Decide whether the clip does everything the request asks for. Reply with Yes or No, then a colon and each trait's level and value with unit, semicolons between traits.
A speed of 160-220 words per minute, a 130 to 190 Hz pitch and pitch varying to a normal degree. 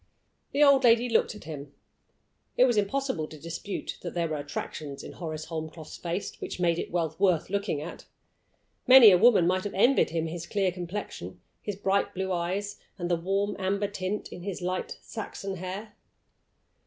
Yes: average, 180 wpm; medium, 185 Hz; average, 3.5 semitones